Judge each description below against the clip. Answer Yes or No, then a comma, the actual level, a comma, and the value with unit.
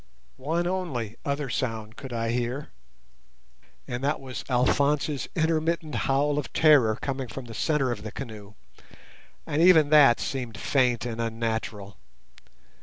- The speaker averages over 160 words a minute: No, slow, 135 wpm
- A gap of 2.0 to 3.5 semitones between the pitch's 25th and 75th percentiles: No, average, 4.3 semitones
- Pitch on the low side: Yes, low, 130 Hz